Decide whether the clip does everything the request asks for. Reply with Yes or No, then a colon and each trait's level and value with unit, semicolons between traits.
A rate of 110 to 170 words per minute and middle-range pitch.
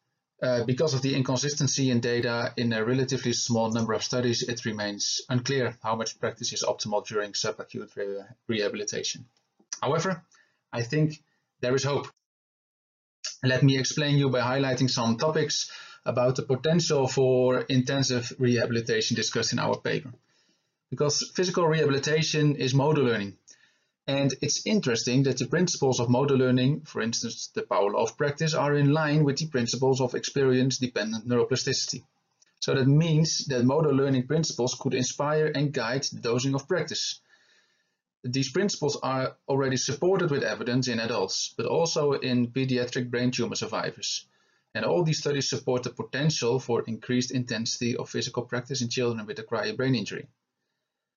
No: average, 155 wpm; low, 130 Hz